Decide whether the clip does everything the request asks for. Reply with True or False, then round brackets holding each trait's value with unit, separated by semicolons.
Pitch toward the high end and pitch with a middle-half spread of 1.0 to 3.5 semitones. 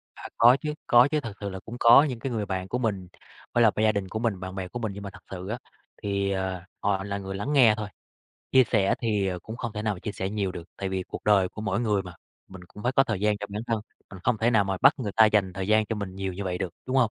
False (105 Hz; 3.1 semitones)